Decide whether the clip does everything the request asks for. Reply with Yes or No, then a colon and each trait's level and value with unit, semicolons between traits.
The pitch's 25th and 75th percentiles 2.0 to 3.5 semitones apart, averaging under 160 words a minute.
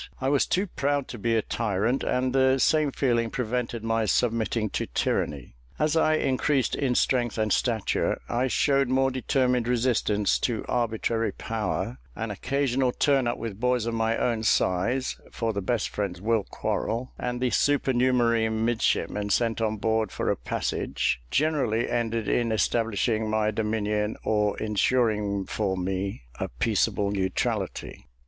Yes: average, 3.0 semitones; average, 150 wpm